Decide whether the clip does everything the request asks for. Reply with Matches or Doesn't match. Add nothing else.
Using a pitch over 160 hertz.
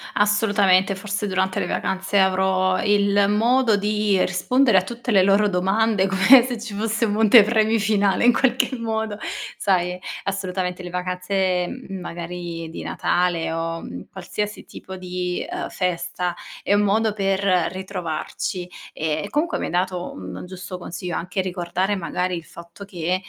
Matches